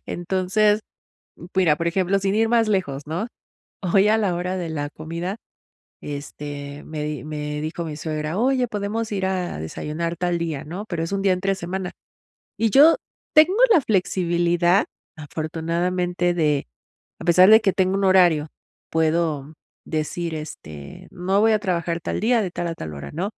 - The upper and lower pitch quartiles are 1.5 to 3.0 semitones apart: No, average, 3.8 semitones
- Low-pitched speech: No, medium, 175 Hz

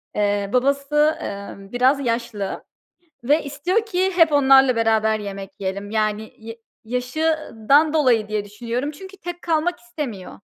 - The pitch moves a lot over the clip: Yes, wide, 5.9 semitones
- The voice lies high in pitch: Yes, very high, 250 Hz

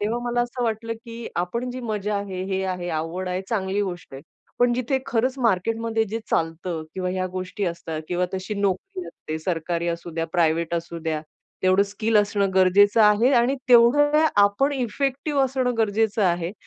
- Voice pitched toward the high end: Yes, high, 205 Hz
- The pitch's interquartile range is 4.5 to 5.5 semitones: Yes, average, 4.8 semitones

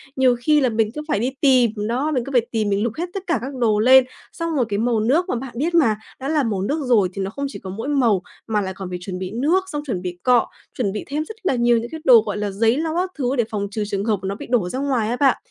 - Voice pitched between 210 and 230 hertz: No, high, 240 Hz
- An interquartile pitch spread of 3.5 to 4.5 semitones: No, average, 5.0 semitones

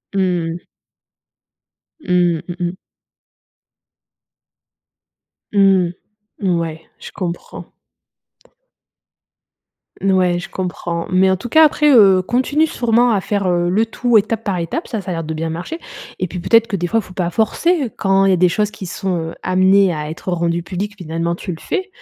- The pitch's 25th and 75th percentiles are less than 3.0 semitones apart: No, average, 3.6 semitones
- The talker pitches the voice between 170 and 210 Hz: Yes, medium, 185 Hz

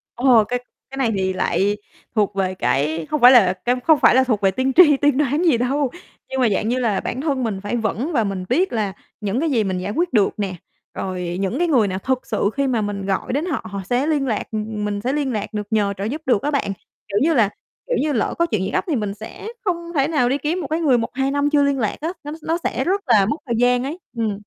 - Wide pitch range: Yes, wide, 5.8 semitones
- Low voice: No, high, 245 Hz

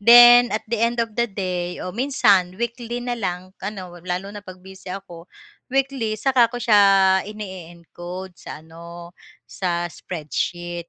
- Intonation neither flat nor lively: Yes, average, 4.8 semitones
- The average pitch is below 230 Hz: Yes, high, 190 Hz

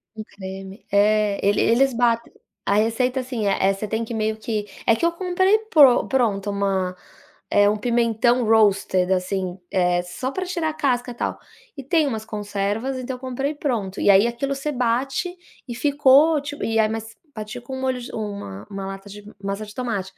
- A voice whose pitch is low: No, high, 225 Hz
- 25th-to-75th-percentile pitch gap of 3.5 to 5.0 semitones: Yes, average, 4.5 semitones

